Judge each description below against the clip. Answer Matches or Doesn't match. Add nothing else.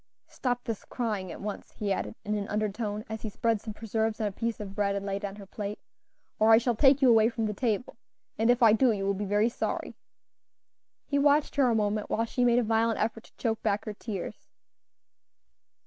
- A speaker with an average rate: Doesn't match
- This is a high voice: Matches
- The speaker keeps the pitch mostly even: Matches